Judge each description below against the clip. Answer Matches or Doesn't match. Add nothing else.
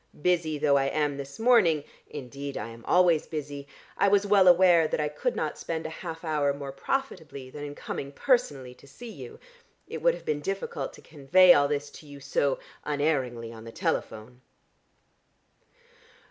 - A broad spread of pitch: Doesn't match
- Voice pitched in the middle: Matches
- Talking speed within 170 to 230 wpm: Matches